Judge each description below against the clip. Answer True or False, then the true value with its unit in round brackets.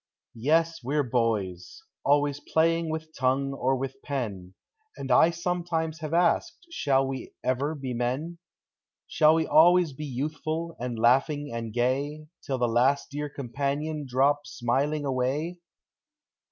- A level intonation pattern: False (3.6 semitones)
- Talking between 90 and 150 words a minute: True (140 wpm)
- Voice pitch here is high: False (140 Hz)